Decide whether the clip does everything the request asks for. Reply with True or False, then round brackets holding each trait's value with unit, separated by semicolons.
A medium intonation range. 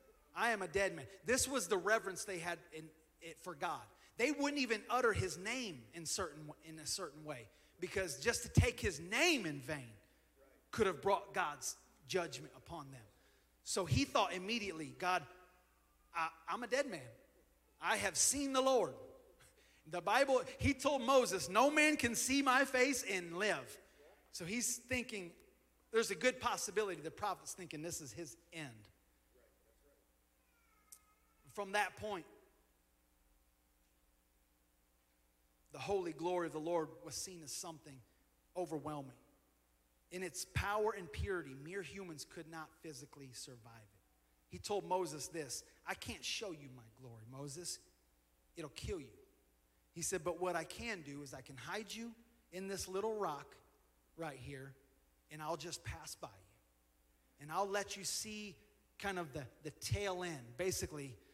False (7.6 semitones)